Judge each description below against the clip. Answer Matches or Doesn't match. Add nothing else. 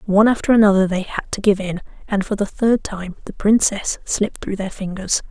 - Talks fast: Matches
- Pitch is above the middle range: Matches